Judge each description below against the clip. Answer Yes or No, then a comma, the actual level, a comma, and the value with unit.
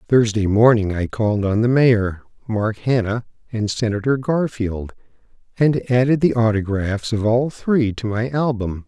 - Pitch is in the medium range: No, low, 115 Hz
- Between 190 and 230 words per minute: No, average, 150 wpm